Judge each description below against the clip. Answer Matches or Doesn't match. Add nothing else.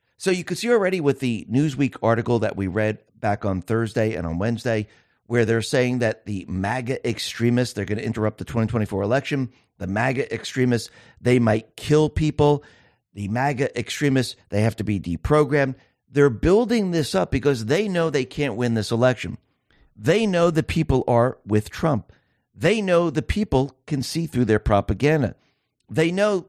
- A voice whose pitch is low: Matches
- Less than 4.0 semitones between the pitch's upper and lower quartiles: Doesn't match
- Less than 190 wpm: Matches